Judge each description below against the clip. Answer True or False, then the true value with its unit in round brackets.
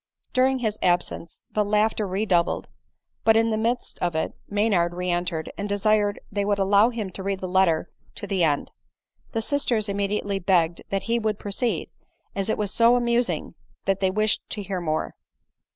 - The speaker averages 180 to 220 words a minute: True (185 wpm)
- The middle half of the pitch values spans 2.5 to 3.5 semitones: True (2.8 semitones)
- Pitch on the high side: True (200 Hz)